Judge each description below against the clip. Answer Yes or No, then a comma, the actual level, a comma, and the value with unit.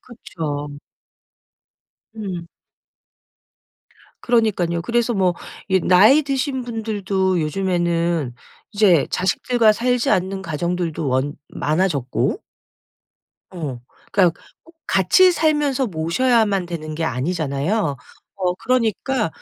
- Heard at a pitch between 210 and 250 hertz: No, medium, 185 Hz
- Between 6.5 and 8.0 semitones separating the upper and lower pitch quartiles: No, wide, 5.5 semitones